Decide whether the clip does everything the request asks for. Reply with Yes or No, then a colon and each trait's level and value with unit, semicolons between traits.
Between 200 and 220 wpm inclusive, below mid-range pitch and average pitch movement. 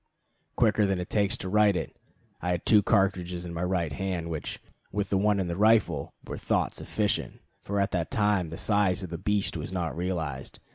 Yes: fast, 205 wpm; very low, 95 Hz; average, 3.0 semitones